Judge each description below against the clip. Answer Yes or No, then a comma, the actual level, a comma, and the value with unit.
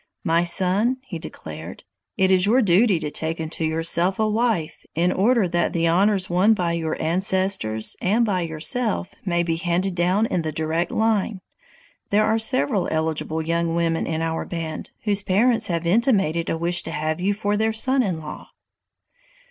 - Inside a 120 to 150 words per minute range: No, average, 175 wpm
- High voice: No, medium, 180 Hz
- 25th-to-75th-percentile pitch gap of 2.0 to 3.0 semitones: No, average, 4.0 semitones